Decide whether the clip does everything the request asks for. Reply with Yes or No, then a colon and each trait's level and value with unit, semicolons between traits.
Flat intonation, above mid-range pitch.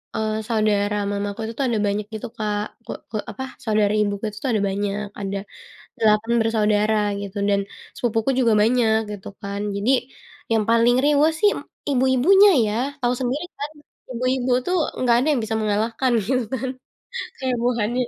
No: average, 3.3 semitones; high, 225 Hz